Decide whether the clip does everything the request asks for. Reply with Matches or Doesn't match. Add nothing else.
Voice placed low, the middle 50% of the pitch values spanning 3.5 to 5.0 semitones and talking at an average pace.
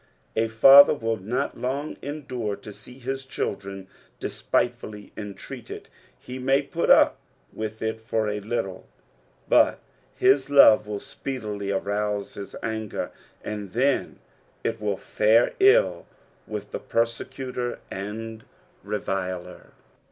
Doesn't match